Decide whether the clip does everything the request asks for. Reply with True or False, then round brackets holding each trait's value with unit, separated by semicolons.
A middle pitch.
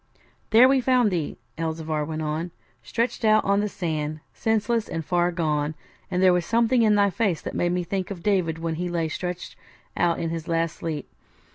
True (175 Hz)